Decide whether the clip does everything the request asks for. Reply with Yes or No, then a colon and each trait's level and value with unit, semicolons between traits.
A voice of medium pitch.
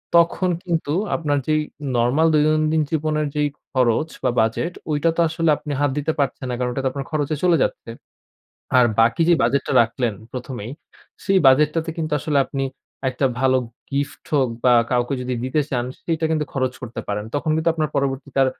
Yes: medium, 145 Hz